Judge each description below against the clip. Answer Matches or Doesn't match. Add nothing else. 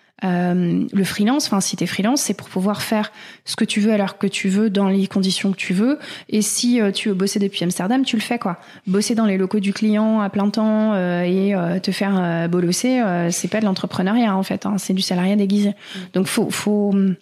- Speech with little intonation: Matches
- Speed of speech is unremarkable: Doesn't match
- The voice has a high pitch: Matches